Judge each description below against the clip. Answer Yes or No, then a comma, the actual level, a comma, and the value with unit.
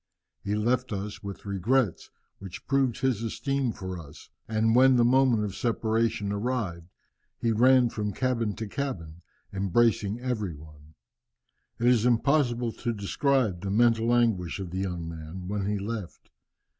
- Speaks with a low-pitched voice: Yes, low, 110 Hz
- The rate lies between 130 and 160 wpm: Yes, average, 150 wpm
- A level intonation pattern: No, average, 3.9 semitones